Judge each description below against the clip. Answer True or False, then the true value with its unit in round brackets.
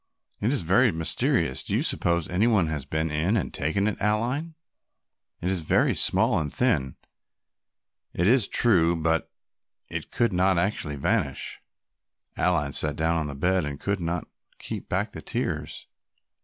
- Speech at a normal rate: True (160 wpm)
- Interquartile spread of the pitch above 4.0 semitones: True (4.7 semitones)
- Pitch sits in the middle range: False (85 Hz)